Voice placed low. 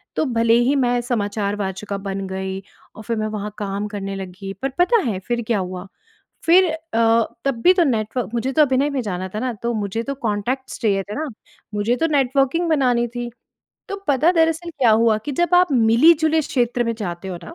No: high, 235 Hz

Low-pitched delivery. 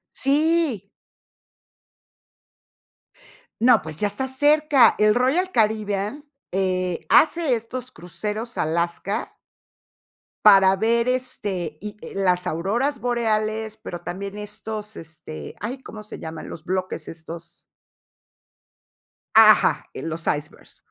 No: high, 210 Hz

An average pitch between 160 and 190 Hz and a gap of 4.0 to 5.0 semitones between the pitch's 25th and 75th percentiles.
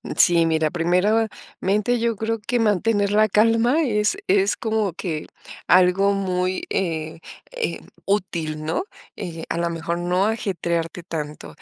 Yes: medium, 185 Hz; average, 4.3 semitones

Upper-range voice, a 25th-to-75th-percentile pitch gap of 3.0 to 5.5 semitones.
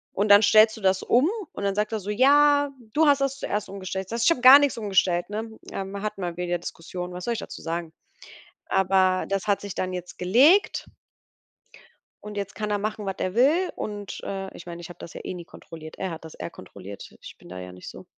Yes: high, 200 Hz; average, 3.7 semitones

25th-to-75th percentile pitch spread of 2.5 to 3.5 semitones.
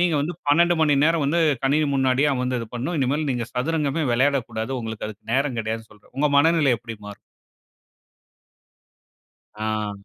No: average, 4.8 semitones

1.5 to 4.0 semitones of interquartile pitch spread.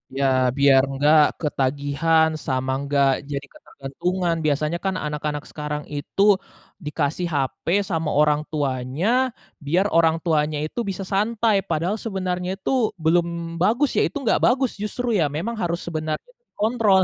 No: average, 4.4 semitones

